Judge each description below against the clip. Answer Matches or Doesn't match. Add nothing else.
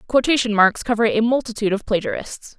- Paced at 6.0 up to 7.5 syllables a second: Matches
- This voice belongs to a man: Doesn't match